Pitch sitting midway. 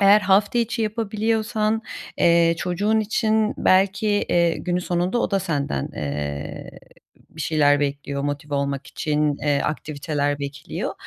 Yes: medium, 170 Hz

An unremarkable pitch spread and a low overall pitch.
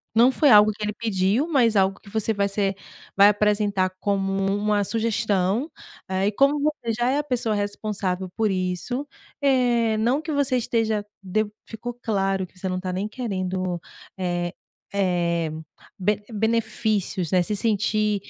No: average, 3.3 semitones; high, 210 Hz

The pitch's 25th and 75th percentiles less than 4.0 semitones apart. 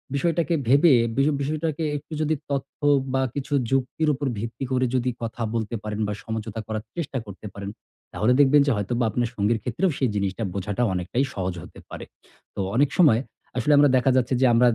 No: average, 4.5 semitones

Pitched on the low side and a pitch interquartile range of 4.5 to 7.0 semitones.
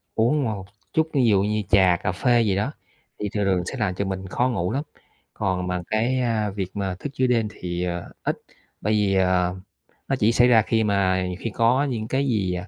No: low, 105 Hz; average, 4.1 semitones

